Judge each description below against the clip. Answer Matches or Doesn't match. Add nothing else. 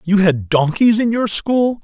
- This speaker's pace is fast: Doesn't match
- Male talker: Matches